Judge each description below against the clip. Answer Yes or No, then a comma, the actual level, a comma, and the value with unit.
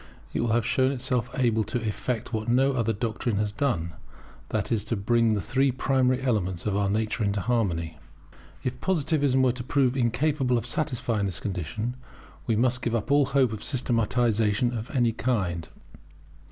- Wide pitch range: No, average, 3.3 semitones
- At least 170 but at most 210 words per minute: Yes, average, 175 wpm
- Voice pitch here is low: Yes, low, 120 Hz